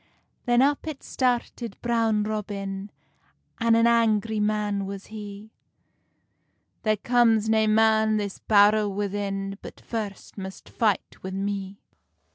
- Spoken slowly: Yes, slow, 120 wpm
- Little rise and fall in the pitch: Yes, narrow, 2.1 semitones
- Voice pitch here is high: Yes, high, 215 Hz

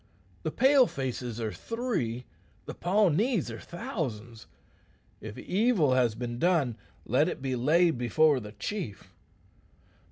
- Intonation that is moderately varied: No, wide, 7.7 semitones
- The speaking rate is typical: No, slow, 125 wpm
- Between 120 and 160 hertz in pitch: Yes, low, 135 Hz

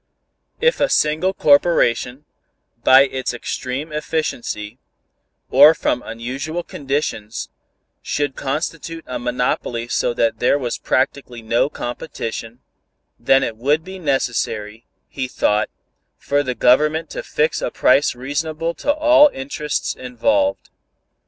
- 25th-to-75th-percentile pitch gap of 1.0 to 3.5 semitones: No, average, 4.3 semitones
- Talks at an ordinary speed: No, slow, 120 wpm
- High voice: No, low, 135 Hz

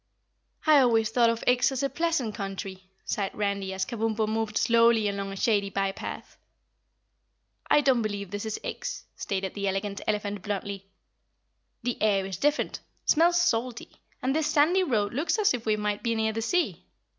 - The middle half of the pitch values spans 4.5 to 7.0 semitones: No, average, 3.8 semitones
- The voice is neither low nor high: No, high, 220 Hz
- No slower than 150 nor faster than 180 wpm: Yes, average, 170 wpm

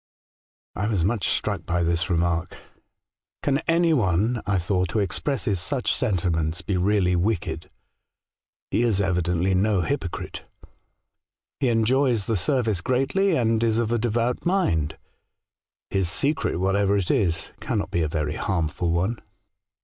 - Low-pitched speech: Yes, low, 100 Hz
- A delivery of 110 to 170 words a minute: Yes, average, 150 wpm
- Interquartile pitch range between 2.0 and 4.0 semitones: No, average, 5.3 semitones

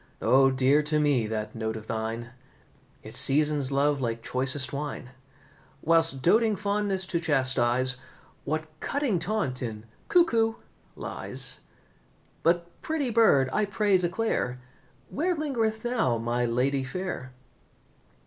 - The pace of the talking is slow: Yes, slow, 120 wpm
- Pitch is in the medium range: Yes, medium, 145 Hz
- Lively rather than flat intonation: Yes, wide, 8.3 semitones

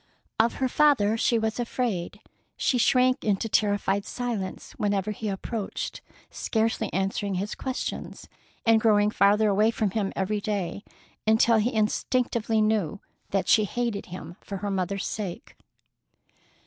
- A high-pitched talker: Yes, high, 210 Hz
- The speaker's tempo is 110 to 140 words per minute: Yes, slow, 135 wpm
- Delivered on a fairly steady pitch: Yes, narrow, 2.3 semitones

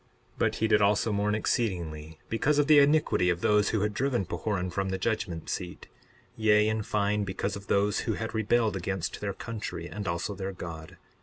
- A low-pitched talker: Yes, low, 100 Hz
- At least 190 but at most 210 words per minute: Yes, average, 200 wpm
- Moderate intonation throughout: Yes, average, 3.1 semitones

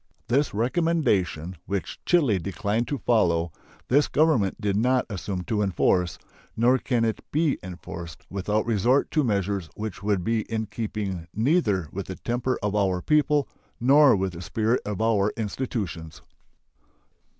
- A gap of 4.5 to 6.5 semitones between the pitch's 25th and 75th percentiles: Yes, average, 4.9 semitones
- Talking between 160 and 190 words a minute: No, average, 145 wpm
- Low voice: Yes, low, 105 Hz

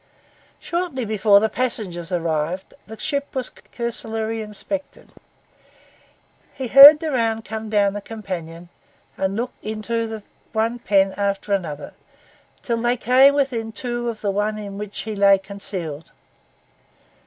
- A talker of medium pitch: No, high, 220 Hz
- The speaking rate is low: Yes, slow, 130 wpm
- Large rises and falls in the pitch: No, average, 3.3 semitones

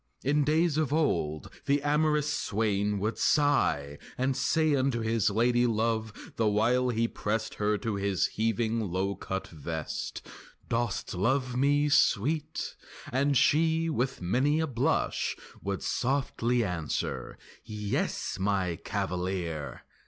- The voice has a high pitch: No, low, 115 Hz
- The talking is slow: Yes, slow, 125 wpm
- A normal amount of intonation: No, wide, 6.0 semitones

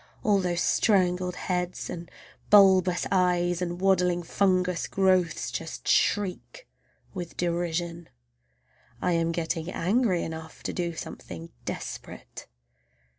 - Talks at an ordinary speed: No, slow, 110 wpm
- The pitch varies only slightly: Yes, narrow, 1.6 semitones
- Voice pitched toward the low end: No, medium, 180 Hz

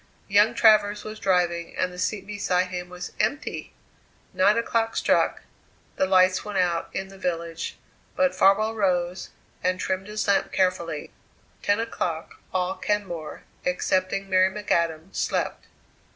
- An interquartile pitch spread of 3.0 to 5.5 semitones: No, narrow, 2.5 semitones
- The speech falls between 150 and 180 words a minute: No, slow, 135 wpm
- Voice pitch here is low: No, high, 190 Hz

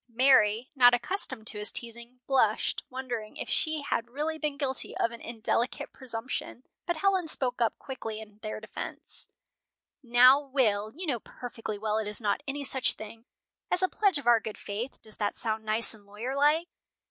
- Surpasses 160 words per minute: Yes, average, 180 wpm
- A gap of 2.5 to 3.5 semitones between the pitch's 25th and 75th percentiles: No, average, 4.0 semitones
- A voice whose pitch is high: Yes, high, 240 Hz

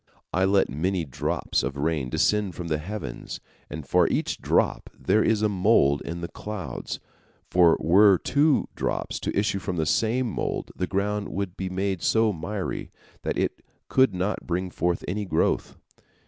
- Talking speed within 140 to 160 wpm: No, average, 170 wpm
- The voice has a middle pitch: No, very low, 95 Hz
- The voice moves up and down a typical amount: Yes, average, 3.8 semitones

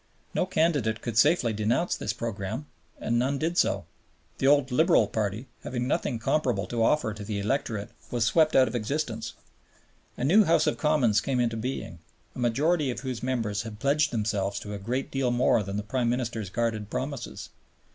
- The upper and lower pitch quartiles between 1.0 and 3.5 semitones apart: No, average, 4.1 semitones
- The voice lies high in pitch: No, low, 120 Hz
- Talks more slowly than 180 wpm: No, average, 185 wpm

